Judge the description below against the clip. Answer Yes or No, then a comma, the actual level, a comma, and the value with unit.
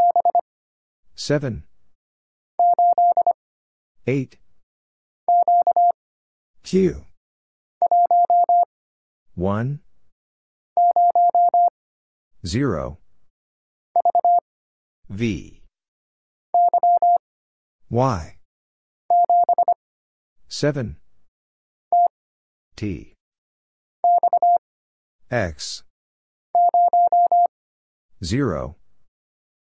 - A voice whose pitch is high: Yes, very high, 350 Hz